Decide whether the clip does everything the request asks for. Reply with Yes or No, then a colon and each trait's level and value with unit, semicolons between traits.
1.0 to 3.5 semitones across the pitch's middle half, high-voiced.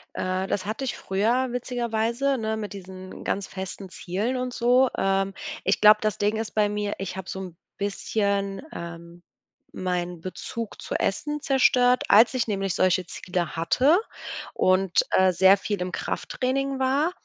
No: average, 4.6 semitones; high, 205 Hz